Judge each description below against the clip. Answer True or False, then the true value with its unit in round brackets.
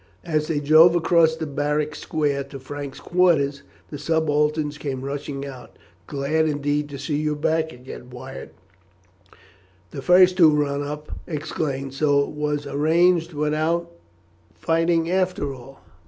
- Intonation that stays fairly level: True (2.2 semitones)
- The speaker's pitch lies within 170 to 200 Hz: False (150 Hz)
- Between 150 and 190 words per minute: False (140 wpm)